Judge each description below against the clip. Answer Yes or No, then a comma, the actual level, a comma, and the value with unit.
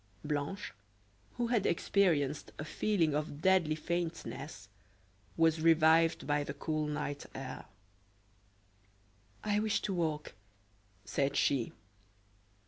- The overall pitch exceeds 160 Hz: No, medium, 155 Hz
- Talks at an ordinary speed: No, slow, 105 wpm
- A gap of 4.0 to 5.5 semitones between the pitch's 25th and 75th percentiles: No, average, 3.1 semitones